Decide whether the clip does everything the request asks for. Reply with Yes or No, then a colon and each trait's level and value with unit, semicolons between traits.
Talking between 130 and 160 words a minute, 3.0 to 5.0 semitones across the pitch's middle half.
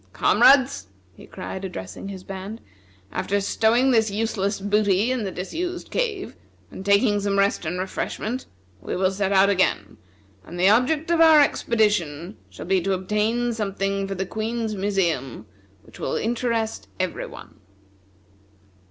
Yes: average, 145 wpm; average, 3.3 semitones